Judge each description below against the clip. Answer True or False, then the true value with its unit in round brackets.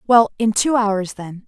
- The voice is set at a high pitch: True (215 Hz)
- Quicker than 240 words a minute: False (205 wpm)